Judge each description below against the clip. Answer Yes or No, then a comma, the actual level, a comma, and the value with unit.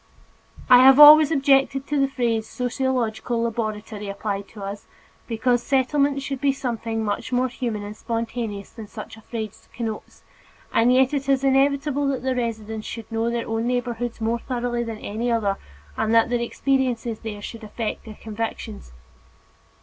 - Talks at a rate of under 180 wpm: Yes, average, 165 wpm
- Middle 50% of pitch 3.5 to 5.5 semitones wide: No, average, 3.0 semitones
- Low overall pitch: No, high, 235 Hz